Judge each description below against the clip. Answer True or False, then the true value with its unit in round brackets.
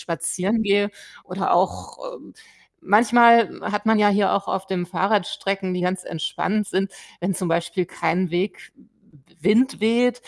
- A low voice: False (195 Hz)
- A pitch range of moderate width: True (3.3 semitones)